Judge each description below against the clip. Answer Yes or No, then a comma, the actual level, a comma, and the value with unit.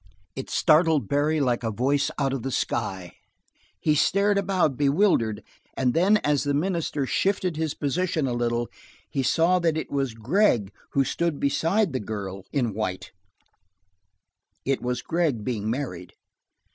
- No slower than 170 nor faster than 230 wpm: No, average, 155 wpm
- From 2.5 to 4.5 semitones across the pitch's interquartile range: No, wide, 5.4 semitones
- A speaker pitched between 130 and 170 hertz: Yes, medium, 140 Hz